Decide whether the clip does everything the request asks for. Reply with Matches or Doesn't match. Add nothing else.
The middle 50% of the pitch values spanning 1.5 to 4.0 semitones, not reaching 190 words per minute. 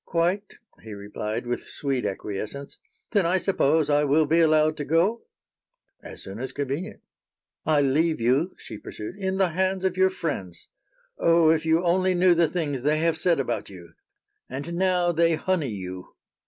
Doesn't match